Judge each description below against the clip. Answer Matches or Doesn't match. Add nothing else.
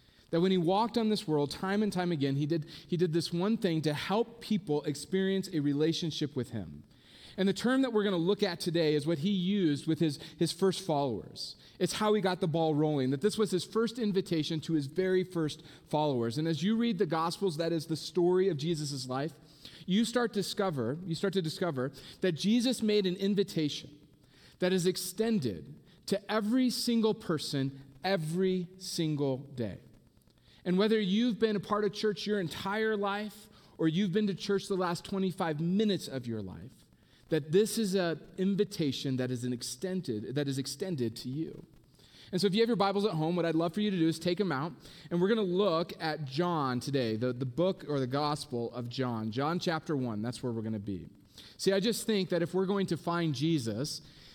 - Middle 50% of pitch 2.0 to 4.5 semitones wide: Doesn't match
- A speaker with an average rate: Doesn't match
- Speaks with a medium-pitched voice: Matches